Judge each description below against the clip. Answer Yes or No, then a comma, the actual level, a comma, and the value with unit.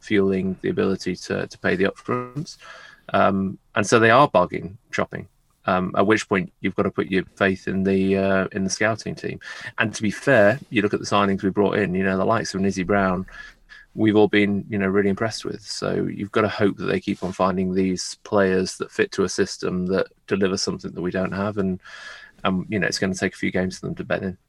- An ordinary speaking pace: No, fast, 245 wpm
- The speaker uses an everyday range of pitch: No, narrow, 1.3 semitones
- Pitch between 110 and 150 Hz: No, very low, 95 Hz